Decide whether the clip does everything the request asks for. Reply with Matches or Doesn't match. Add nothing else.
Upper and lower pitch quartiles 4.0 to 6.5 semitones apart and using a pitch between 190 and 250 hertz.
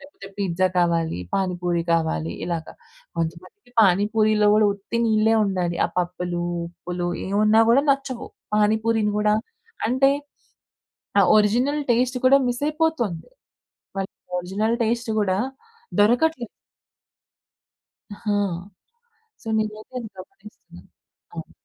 Matches